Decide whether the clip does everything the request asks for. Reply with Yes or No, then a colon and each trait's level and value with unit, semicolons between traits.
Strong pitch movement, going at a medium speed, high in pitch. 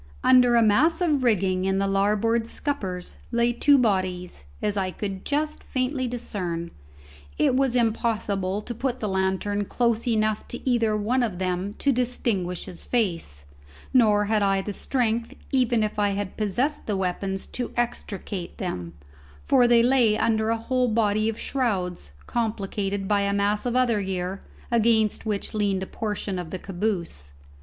No: average, 3.7 semitones; average, 165 wpm; high, 210 Hz